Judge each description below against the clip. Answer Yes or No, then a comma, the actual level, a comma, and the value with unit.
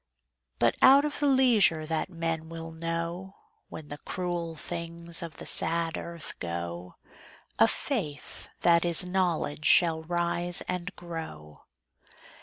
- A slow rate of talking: Yes, slow, 130 wpm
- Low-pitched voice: No, medium, 170 Hz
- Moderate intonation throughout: No, narrow, 1.7 semitones